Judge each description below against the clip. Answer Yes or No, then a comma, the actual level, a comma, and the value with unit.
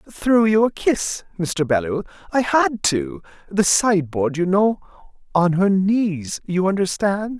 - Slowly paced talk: Yes, slow, 120 wpm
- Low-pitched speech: No, high, 190 Hz